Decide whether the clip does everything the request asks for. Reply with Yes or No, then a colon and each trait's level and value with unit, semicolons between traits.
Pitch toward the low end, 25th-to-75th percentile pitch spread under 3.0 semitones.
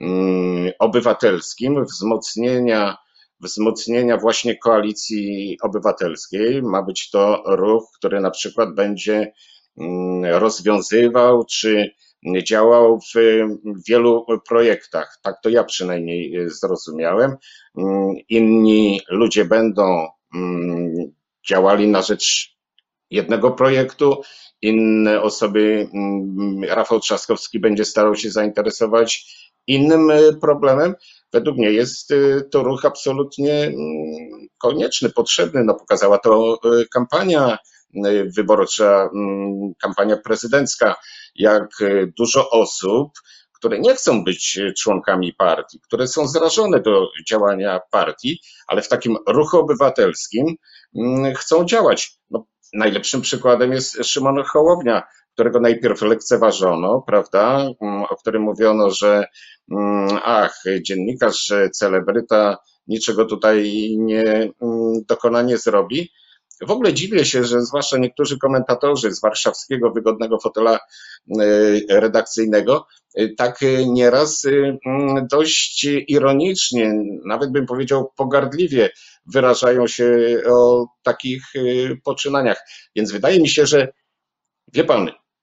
No: low, 115 Hz; average, 4.1 semitones